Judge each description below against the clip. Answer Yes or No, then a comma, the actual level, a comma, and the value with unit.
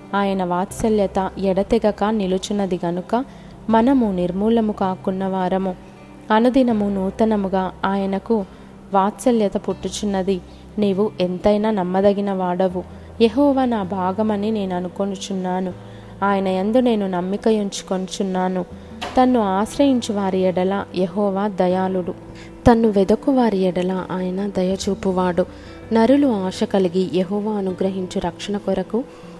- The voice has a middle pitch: No, high, 195 Hz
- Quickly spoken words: No, average, 95 wpm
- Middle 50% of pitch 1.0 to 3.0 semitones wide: Yes, narrow, 2.4 semitones